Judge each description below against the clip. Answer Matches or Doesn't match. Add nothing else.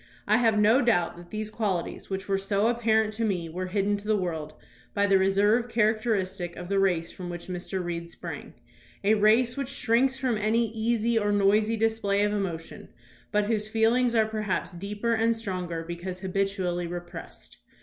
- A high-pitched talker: Matches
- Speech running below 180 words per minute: Doesn't match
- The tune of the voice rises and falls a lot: Doesn't match